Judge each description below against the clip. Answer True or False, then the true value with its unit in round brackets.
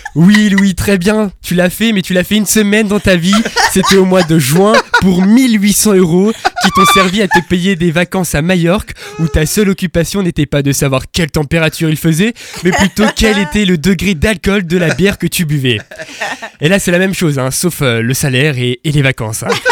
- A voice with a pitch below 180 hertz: False (185 Hz)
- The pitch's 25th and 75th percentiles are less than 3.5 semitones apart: False (4.0 semitones)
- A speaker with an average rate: False (225 wpm)